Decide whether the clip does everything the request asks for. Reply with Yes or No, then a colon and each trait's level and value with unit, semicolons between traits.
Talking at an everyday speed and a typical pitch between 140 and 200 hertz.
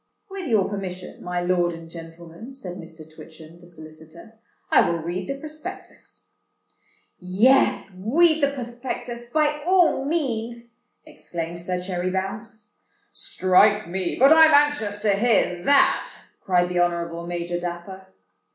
No: slow, 130 wpm; high, 190 Hz